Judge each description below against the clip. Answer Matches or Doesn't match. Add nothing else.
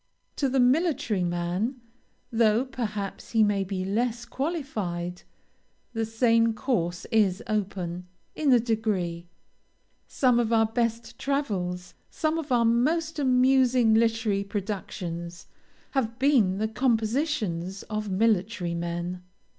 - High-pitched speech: Matches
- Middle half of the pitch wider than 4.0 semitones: Matches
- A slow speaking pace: Matches